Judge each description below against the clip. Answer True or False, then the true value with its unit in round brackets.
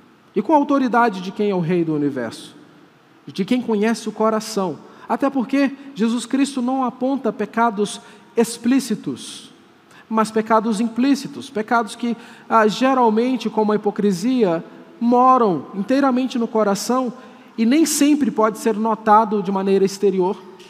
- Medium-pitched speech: False (225 Hz)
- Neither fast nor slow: True (135 wpm)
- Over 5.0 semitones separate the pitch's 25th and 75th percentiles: False (3.3 semitones)